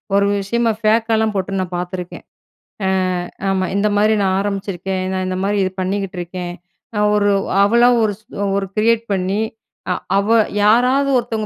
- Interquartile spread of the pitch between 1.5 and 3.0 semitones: Yes, average, 2.7 semitones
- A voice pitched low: No, high, 200 Hz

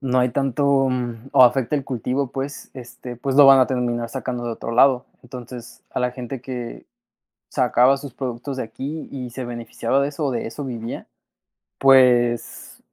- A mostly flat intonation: Yes, narrow, 2.0 semitones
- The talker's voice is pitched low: Yes, low, 125 Hz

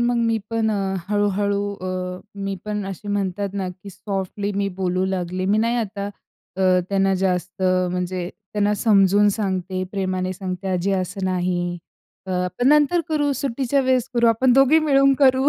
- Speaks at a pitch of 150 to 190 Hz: No, high, 200 Hz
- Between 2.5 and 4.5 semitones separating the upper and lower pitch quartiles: Yes, average, 3.5 semitones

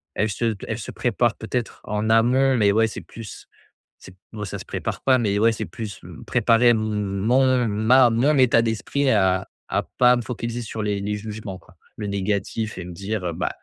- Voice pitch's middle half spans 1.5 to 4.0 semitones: Yes, average, 2.7 semitones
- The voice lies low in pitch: Yes, low, 110 Hz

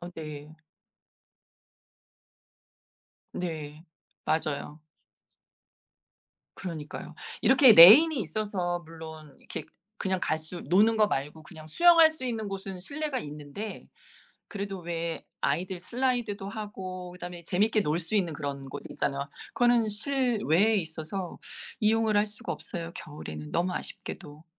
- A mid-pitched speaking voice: Yes, medium, 180 Hz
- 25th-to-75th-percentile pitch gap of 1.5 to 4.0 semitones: No, average, 5.3 semitones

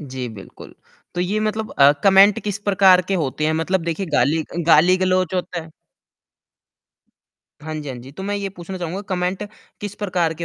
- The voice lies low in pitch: No, medium, 180 Hz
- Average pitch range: Yes, average, 3.6 semitones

